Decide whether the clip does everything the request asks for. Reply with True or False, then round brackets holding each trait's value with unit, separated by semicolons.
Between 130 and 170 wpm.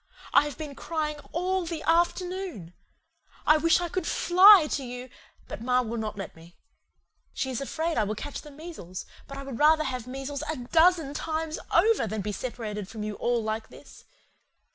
False (190 wpm)